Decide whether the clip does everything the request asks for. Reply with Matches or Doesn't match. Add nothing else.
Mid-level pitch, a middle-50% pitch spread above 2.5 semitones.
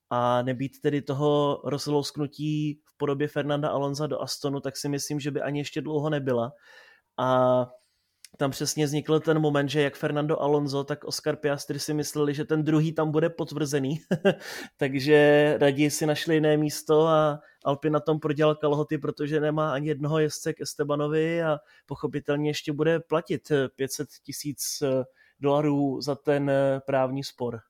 Doesn't match